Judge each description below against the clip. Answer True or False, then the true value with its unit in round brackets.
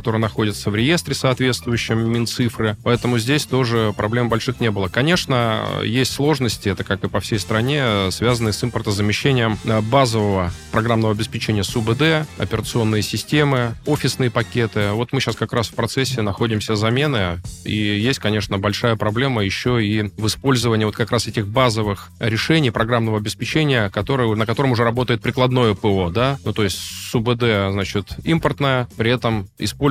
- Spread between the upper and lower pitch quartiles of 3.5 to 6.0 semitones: False (2.9 semitones)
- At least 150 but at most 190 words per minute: True (155 wpm)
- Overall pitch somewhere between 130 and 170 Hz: False (115 Hz)